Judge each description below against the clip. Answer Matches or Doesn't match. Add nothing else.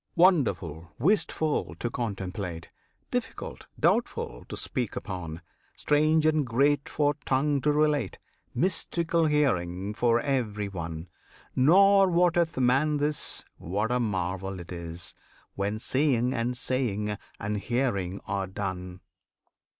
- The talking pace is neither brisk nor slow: Doesn't match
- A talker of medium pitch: Doesn't match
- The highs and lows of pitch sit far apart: Matches